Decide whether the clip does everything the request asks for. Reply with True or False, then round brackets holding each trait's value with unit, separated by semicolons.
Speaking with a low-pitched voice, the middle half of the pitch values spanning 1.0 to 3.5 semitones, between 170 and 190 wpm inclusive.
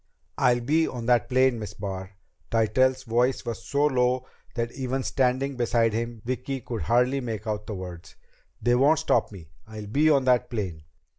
True (120 Hz; 3.1 semitones; 175 wpm)